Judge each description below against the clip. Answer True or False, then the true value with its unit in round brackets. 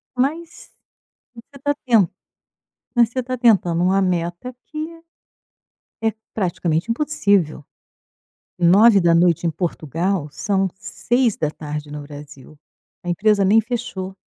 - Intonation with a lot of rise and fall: True (5.8 semitones)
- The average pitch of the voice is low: False (190 Hz)